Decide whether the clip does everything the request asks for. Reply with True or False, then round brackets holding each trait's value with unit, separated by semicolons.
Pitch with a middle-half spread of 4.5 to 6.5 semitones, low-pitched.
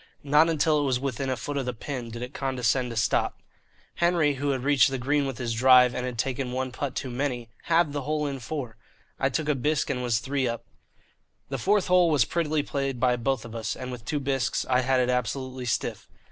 False (2.7 semitones; 130 Hz)